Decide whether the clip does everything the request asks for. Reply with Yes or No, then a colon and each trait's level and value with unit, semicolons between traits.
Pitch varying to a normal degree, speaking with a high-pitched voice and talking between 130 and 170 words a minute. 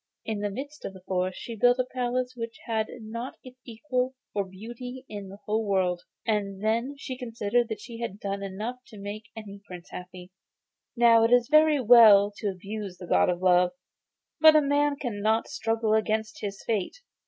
No: average, 3.7 semitones; high, 220 Hz; average, 190 wpm